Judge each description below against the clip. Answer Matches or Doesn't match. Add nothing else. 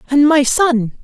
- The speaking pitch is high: Matches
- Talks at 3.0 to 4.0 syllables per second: Matches